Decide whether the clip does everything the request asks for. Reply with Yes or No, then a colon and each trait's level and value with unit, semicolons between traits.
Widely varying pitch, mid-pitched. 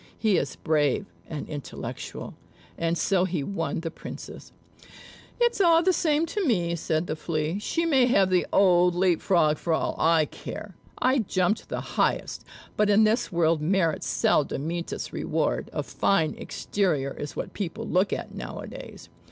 No: average, 4.7 semitones; medium, 180 Hz